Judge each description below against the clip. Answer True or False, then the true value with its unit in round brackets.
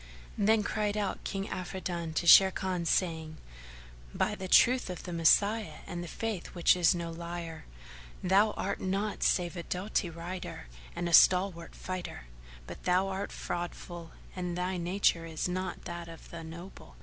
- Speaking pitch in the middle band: True (180 Hz)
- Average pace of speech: True (160 wpm)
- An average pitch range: False (2.2 semitones)